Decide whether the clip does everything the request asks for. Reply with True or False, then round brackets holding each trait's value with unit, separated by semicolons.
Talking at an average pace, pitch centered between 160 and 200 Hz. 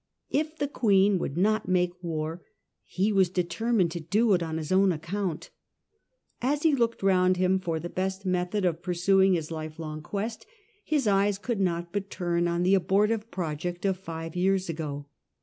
True (180 wpm; 185 Hz)